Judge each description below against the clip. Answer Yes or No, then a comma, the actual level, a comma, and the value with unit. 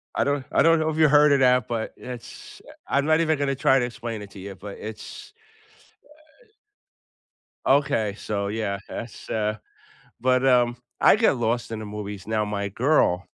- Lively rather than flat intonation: No, average, 4.9 semitones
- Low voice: Yes, low, 120 Hz